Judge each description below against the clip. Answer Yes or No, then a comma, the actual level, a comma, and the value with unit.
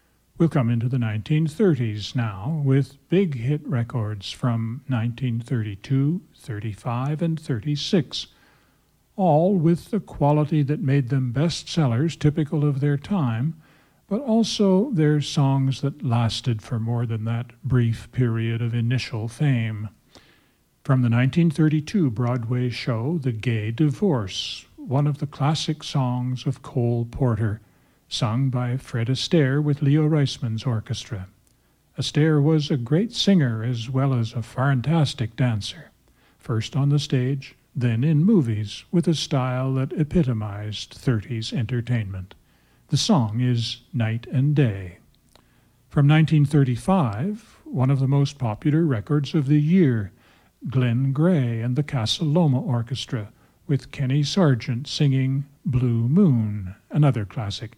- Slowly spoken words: Yes, slow, 130 wpm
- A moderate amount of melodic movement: Yes, average, 4.2 semitones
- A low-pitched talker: Yes, low, 130 Hz